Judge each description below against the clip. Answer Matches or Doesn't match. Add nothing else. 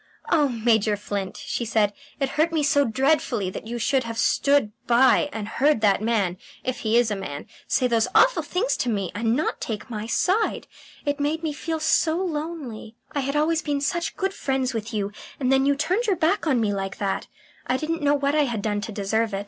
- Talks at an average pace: Doesn't match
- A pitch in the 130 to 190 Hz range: Doesn't match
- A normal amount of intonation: Doesn't match